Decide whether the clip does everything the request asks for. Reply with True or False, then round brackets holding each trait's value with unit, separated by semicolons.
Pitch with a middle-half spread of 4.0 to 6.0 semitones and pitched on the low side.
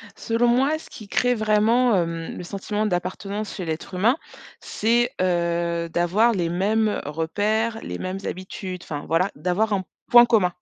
False (4.3 semitones; 200 Hz)